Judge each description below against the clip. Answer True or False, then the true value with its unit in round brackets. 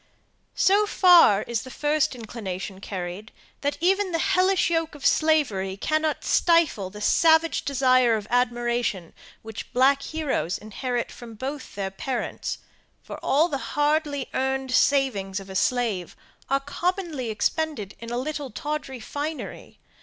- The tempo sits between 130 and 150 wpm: True (140 wpm)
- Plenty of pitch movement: True (6.1 semitones)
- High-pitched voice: True (265 Hz)